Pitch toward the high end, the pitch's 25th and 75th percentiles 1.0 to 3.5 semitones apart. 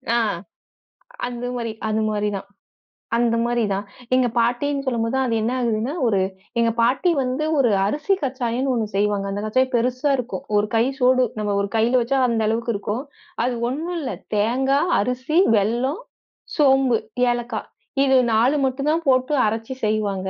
Yes: high, 240 Hz; average, 3.2 semitones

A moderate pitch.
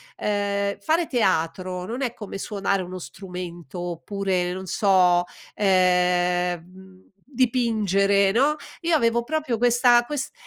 No: high, 195 Hz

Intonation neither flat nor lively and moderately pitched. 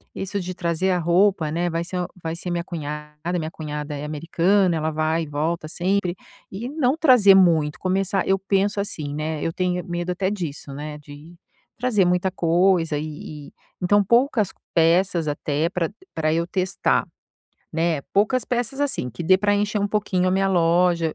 Yes: average, 3.4 semitones; medium, 175 Hz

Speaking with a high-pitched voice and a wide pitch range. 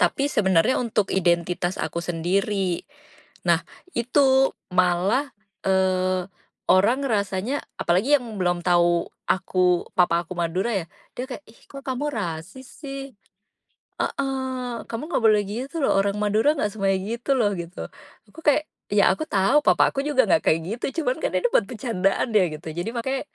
Yes: high, 205 Hz; wide, 6.2 semitones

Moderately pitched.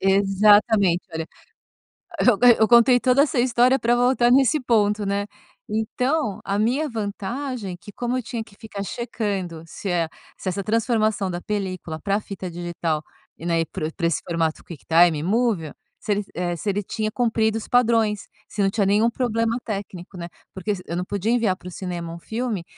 No: high, 205 Hz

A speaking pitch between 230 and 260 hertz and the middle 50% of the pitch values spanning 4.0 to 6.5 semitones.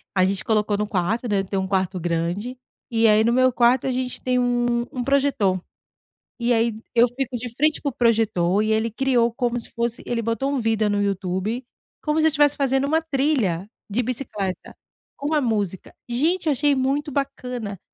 Yes: high, 235 Hz; average, 4.4 semitones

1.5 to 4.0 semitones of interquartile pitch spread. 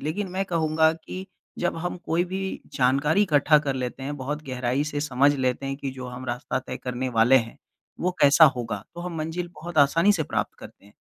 No: average, 4.4 semitones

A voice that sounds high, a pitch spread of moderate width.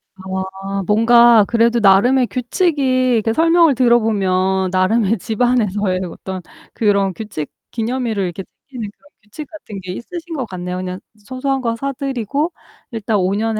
Yes: high, 225 Hz; average, 4.7 semitones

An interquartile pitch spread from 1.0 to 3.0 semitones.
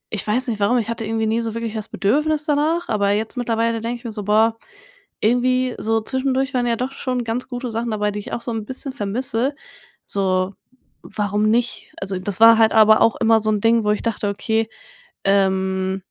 Yes: average, 2.7 semitones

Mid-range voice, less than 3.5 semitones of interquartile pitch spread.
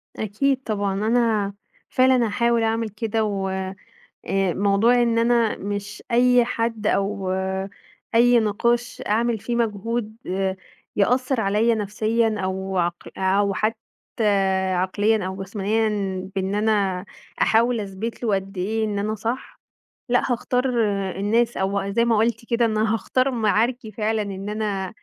No: high, 220 Hz; average, 2.8 semitones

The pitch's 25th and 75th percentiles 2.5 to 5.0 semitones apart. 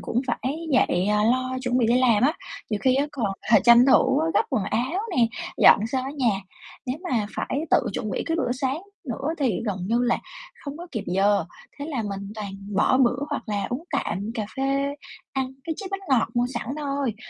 Yes: average, 4.0 semitones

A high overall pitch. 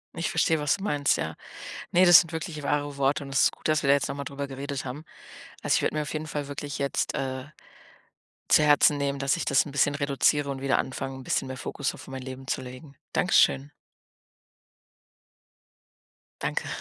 No: medium, 140 Hz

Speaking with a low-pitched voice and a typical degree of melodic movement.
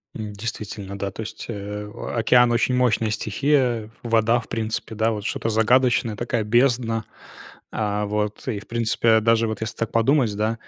No: low, 115 Hz; narrow, 1.9 semitones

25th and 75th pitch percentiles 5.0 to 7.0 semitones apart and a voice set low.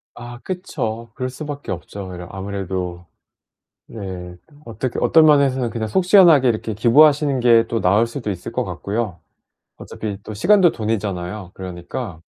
Yes: wide, 5.5 semitones; low, 110 Hz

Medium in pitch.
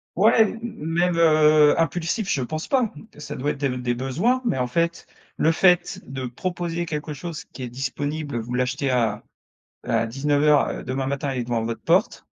Yes: medium, 145 Hz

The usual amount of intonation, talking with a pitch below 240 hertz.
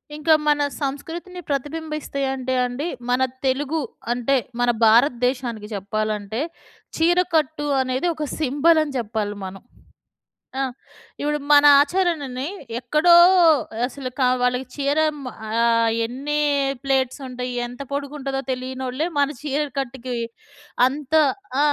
No: average, 3.2 semitones; very high, 270 Hz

